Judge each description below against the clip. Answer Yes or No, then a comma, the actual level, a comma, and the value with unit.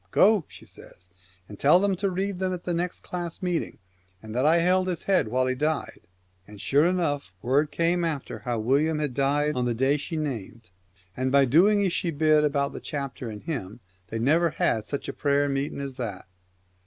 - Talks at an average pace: No, fast, 215 wpm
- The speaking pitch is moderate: Yes, medium, 145 Hz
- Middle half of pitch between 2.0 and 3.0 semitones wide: No, average, 5.0 semitones